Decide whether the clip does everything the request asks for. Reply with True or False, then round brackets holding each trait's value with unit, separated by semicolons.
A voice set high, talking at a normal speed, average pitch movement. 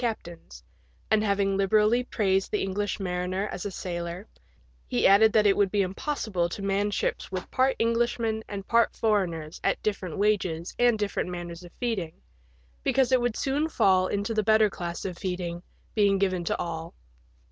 True (195 Hz; 170 wpm; 3.4 semitones)